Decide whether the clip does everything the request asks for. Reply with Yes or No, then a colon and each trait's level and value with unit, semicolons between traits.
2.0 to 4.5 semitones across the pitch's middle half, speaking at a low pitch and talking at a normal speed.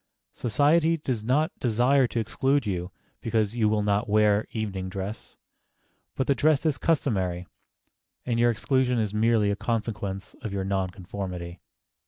Yes: average, 4.2 semitones; low, 110 Hz; average, 150 wpm